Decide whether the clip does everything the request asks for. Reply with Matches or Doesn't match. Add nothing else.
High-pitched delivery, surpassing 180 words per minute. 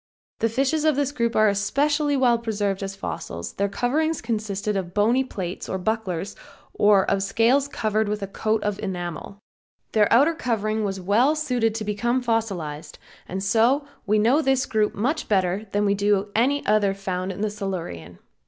Doesn't match